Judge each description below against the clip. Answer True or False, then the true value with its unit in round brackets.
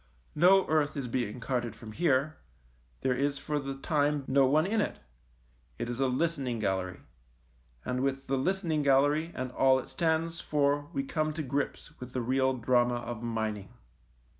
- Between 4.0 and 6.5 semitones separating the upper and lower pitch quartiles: False (3.6 semitones)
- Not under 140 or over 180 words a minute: True (170 wpm)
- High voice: False (135 Hz)